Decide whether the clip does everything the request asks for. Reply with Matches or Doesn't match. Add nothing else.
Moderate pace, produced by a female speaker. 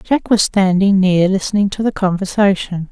Matches